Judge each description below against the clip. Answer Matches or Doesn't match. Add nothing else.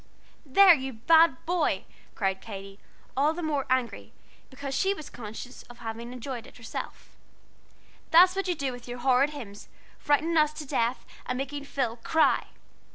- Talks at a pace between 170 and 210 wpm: Doesn't match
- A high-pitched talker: Matches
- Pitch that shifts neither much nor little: Matches